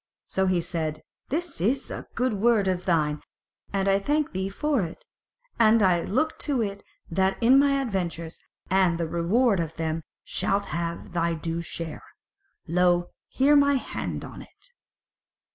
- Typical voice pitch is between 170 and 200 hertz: Yes, high, 190 Hz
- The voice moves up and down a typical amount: No, wide, 6.0 semitones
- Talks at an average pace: Yes, average, 160 wpm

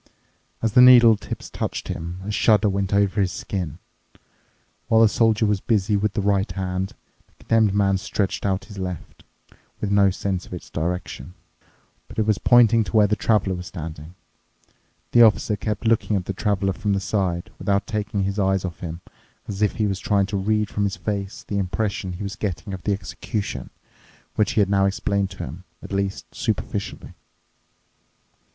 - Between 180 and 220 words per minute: Yes, average, 185 wpm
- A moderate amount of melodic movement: No, narrow, 2.0 semitones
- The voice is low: Yes, low, 100 Hz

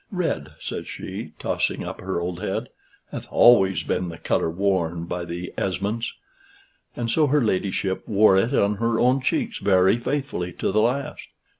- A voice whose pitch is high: No, low, 100 Hz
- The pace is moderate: Yes, average, 165 wpm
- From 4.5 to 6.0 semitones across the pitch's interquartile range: Yes, average, 5.0 semitones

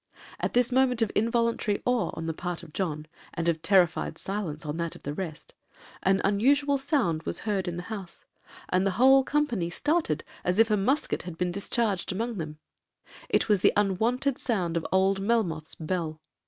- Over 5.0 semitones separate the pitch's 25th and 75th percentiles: Yes, wide, 5.5 semitones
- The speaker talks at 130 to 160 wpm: No, average, 180 wpm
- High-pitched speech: Yes, high, 195 Hz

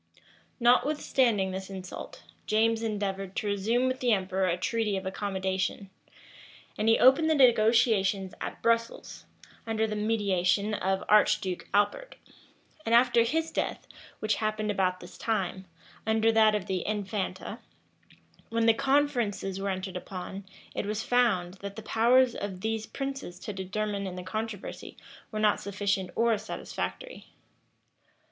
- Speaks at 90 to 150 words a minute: Yes, average, 140 wpm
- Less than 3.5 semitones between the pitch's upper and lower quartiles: Yes, average, 3.0 semitones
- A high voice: Yes, high, 210 Hz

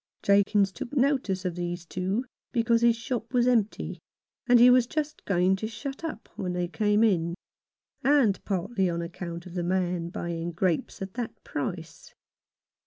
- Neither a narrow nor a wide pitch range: Yes, average, 5.0 semitones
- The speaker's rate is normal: Yes, average, 165 wpm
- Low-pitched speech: No, high, 200 Hz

